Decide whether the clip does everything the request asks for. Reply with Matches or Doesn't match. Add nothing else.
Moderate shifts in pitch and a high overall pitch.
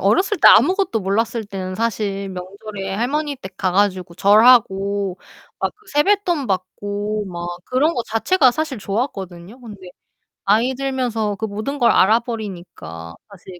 Matches